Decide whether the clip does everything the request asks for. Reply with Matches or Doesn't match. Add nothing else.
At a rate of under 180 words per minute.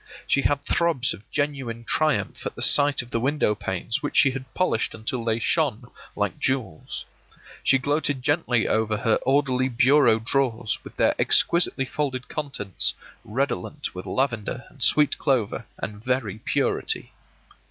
Matches